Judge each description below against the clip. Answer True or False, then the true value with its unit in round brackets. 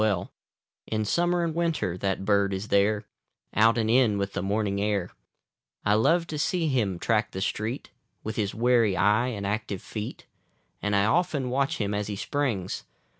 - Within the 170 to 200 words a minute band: True (190 wpm)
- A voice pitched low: True (110 Hz)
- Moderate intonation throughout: True (4.0 semitones)